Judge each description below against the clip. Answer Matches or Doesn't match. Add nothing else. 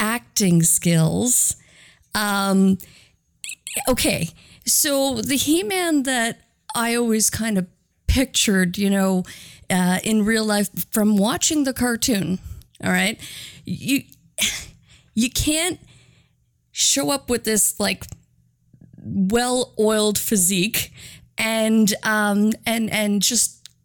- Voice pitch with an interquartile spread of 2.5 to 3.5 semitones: Doesn't match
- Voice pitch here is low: Doesn't match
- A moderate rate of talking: Doesn't match